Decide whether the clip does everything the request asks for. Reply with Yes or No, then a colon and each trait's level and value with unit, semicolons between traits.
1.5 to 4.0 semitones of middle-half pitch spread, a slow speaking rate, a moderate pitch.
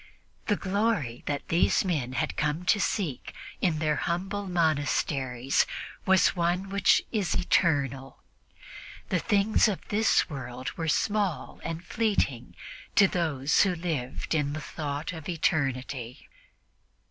No: average, 5.3 semitones; slow, 125 wpm; medium, 160 Hz